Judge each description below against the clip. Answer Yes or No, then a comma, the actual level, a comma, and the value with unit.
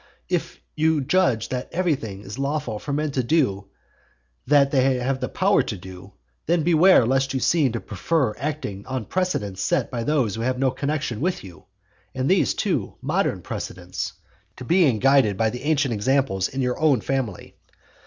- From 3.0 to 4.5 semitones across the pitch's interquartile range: No, wide, 5.4 semitones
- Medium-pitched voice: No, low, 130 Hz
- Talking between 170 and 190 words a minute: Yes, average, 175 wpm